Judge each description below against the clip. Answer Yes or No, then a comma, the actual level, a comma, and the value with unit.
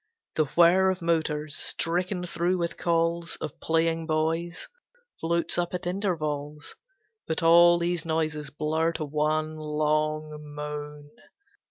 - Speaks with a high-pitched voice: No, medium, 160 Hz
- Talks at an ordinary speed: No, slow, 125 wpm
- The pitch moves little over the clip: Yes, narrow, 2.0 semitones